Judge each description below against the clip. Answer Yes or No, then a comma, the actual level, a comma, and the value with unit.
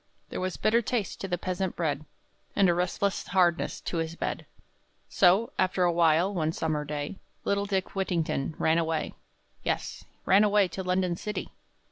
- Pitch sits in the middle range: Yes, medium, 180 Hz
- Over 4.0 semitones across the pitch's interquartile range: No, average, 3.0 semitones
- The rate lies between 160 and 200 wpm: Yes, average, 165 wpm